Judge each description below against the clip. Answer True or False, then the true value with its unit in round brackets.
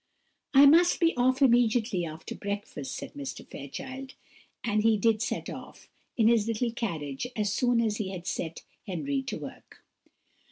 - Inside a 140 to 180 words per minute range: True (160 wpm)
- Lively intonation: False (4.3 semitones)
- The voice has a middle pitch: False (230 Hz)